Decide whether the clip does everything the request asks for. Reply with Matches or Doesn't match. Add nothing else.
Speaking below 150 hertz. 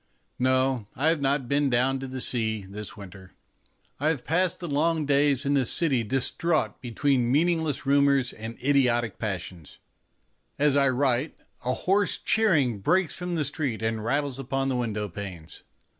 Matches